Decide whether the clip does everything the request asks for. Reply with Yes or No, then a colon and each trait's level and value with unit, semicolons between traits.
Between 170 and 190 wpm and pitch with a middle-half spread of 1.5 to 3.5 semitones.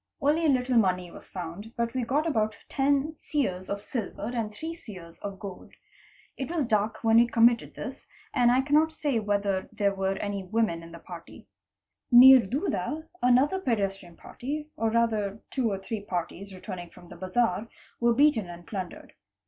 No: average, 180 wpm; average, 5.3 semitones